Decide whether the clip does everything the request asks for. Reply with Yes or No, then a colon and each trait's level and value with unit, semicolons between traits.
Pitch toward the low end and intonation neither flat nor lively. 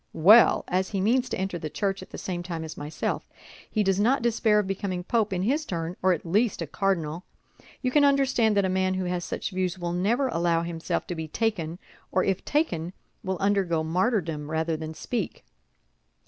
No: medium, 185 Hz; average, 4.0 semitones